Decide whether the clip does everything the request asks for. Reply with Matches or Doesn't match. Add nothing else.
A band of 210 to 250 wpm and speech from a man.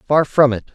Matches